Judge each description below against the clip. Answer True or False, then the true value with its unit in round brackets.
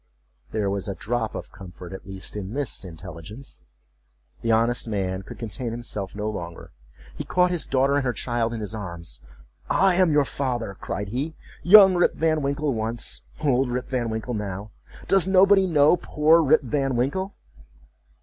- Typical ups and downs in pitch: False (6.5 semitones)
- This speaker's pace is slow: False (160 wpm)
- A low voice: True (120 Hz)